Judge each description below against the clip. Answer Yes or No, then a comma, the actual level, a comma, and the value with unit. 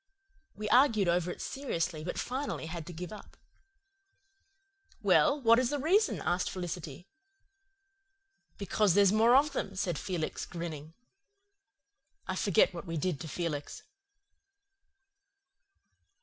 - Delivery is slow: Yes, slow, 125 wpm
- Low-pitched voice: No, medium, 185 Hz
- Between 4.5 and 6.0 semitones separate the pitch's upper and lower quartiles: Yes, wide, 5.5 semitones